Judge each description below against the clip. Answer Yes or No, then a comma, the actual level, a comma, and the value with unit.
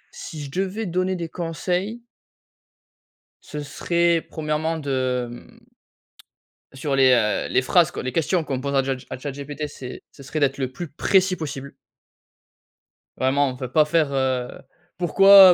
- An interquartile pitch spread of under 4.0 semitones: No, average, 4.4 semitones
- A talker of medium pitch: Yes, medium, 150 Hz